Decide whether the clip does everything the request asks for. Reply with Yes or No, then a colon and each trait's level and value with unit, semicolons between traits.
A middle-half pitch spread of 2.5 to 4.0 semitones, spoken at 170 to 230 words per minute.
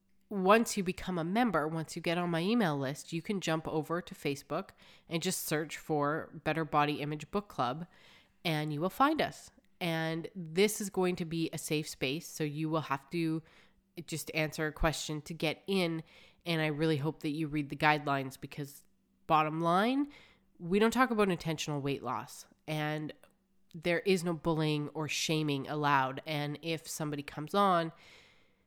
Yes: average, 2.8 semitones; average, 180 wpm